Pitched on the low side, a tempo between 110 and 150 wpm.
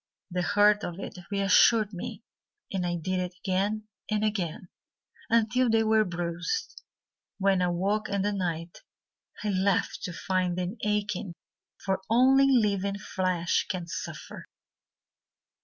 No: high, 195 Hz; slow, 135 wpm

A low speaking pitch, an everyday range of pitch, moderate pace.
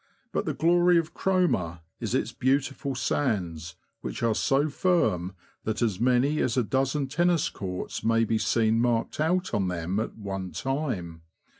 No: low, 120 Hz; wide, 7.2 semitones; average, 160 wpm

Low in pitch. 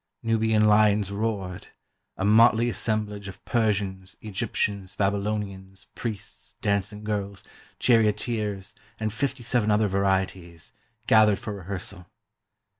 Yes: low, 105 Hz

